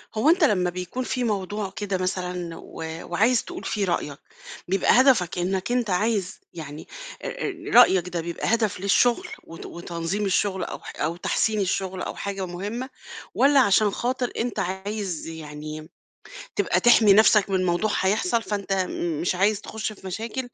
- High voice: Yes, high, 195 Hz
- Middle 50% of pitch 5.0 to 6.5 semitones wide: No, average, 3.7 semitones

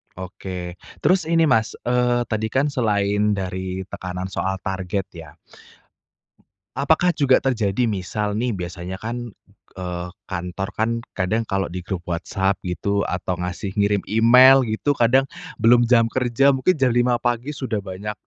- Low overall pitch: Yes, low, 105 Hz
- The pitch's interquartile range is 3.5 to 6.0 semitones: Yes, average, 4.7 semitones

